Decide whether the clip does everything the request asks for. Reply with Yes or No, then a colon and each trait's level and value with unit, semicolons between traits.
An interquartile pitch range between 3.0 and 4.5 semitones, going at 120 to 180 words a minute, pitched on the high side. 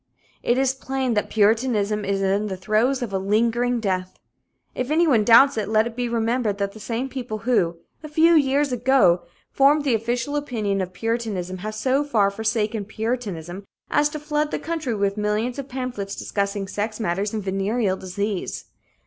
Yes: average, 4.2 semitones; average, 175 wpm; high, 225 Hz